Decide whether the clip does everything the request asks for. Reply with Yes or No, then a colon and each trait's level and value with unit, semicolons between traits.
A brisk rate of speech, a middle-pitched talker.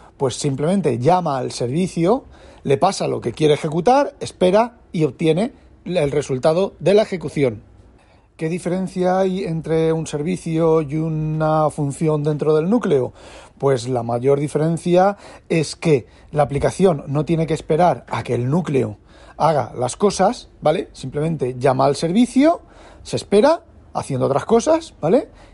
No: average, 145 wpm; medium, 160 Hz